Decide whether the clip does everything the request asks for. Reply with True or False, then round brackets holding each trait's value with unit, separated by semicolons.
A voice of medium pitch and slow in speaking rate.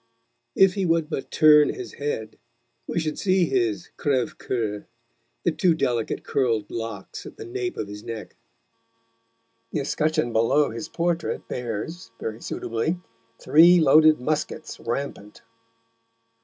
True (145 Hz; 130 wpm)